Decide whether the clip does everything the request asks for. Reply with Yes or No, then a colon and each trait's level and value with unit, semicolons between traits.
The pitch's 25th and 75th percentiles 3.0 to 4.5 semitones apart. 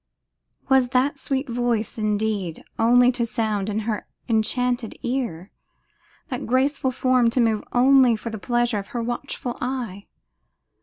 No: narrow, 2.6 semitones